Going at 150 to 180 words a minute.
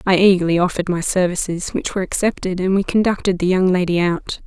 No: average, 200 wpm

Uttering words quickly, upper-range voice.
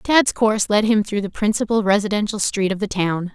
Yes: fast, 215 wpm; high, 210 Hz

